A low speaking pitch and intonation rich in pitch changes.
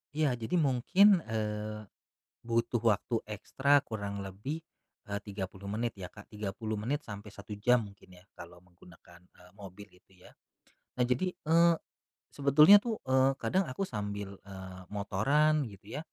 Yes: low, 110 Hz; wide, 5.8 semitones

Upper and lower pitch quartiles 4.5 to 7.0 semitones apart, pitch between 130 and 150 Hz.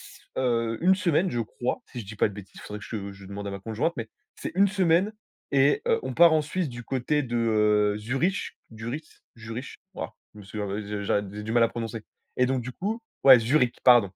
No: wide, 5.6 semitones; low, 120 Hz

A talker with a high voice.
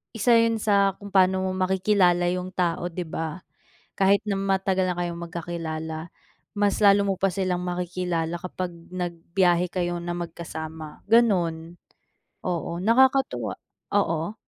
No: medium, 180 Hz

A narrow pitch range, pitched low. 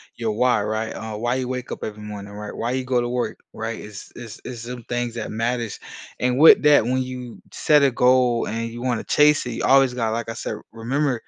Yes: narrow, 2.2 semitones; low, 120 Hz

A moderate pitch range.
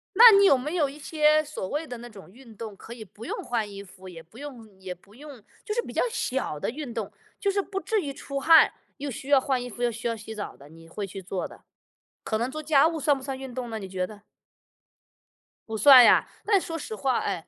No: wide, 5.8 semitones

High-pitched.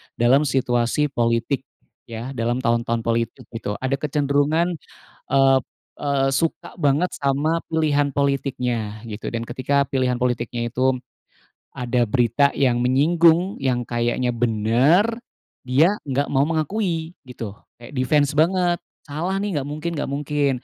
No: low, 135 Hz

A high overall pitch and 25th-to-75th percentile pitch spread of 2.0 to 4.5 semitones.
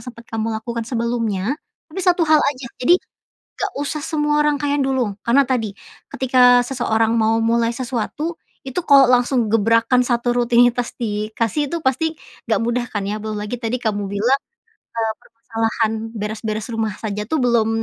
Yes: high, 240 Hz; average, 3.3 semitones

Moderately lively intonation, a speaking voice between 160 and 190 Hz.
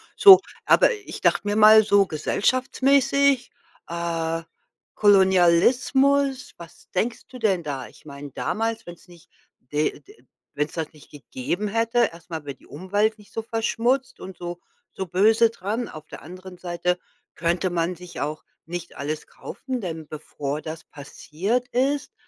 No: wide, 5.8 semitones; medium, 185 Hz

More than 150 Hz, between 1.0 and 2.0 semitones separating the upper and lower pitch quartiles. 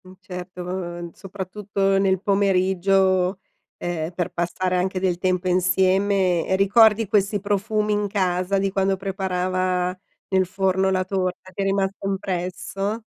Yes: high, 190 Hz; narrow, 1.3 semitones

